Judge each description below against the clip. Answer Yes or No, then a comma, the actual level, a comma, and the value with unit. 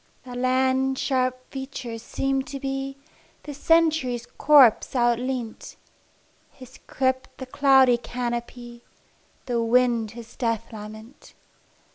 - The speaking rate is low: Yes, slow, 105 wpm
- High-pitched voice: Yes, very high, 255 Hz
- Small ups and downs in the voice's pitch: Yes, narrow, 2.0 semitones